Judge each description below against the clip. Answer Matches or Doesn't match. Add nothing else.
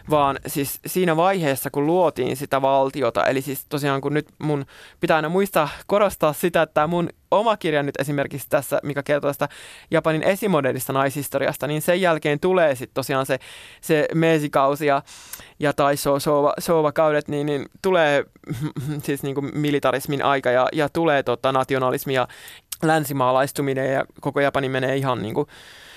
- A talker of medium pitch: Matches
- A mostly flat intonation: Matches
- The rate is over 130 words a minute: Matches